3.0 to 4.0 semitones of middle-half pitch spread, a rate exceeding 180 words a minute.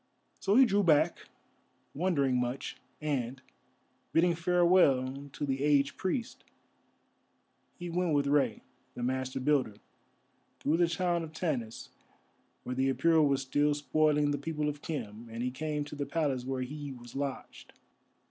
No: average, 3.6 semitones; average, 150 wpm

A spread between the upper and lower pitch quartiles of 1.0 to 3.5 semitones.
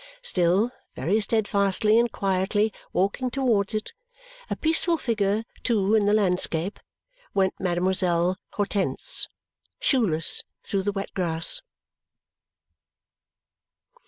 Yes: average, 2.9 semitones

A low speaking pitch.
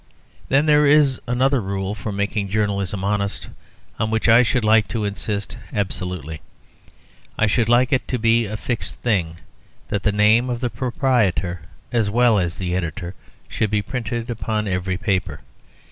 Yes: low, 105 Hz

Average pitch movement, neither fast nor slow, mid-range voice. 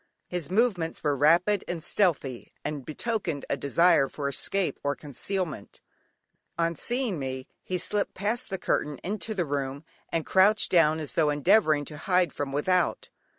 Yes: average, 4.8 semitones; average, 160 wpm; medium, 165 Hz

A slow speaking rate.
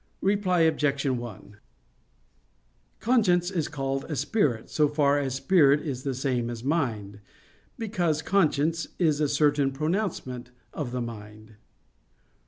Yes: slow, 125 wpm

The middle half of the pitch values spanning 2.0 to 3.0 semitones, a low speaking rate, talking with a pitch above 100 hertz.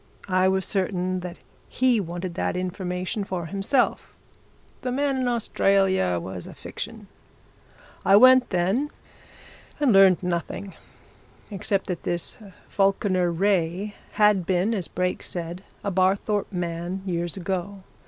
Yes: narrow, 2.4 semitones; slow, 125 wpm; high, 190 Hz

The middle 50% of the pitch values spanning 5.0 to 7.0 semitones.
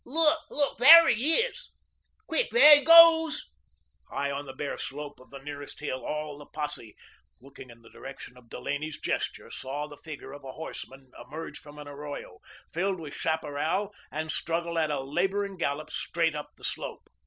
Yes: wide, 5.6 semitones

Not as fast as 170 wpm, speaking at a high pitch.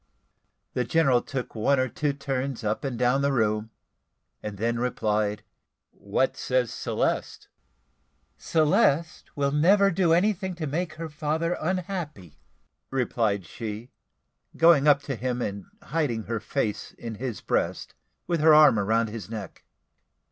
No: average, 140 wpm; low, 135 Hz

